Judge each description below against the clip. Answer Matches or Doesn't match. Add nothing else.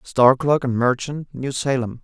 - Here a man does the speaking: Matches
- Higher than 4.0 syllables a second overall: Matches